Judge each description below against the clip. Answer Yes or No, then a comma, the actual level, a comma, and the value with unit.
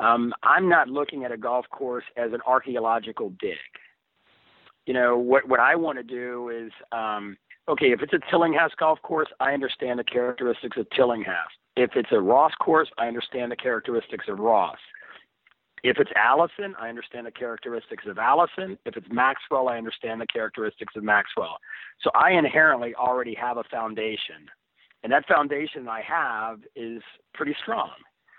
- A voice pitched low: Yes, low, 125 Hz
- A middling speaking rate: Yes, average, 165 wpm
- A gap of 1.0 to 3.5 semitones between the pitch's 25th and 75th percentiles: Yes, average, 3.1 semitones